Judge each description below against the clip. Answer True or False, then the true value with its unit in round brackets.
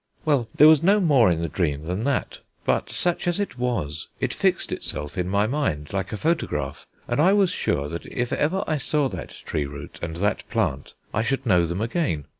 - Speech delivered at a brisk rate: True (215 wpm)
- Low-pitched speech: True (110 Hz)